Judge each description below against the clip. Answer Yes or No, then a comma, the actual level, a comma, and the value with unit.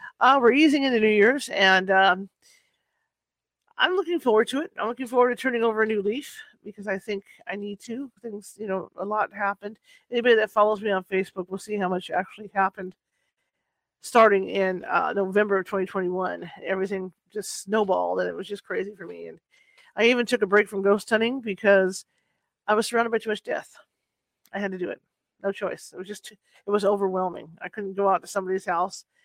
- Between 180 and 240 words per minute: Yes, average, 200 wpm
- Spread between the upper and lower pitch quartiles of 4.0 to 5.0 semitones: No, average, 3.4 semitones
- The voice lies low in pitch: No, high, 205 Hz